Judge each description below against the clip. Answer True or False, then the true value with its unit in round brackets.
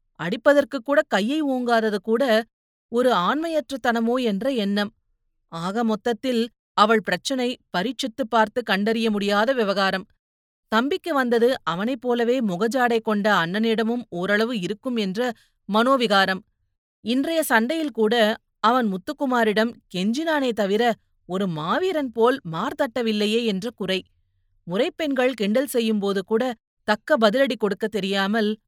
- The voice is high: True (225 Hz)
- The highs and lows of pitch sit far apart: False (3.7 semitones)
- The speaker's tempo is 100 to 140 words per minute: True (110 wpm)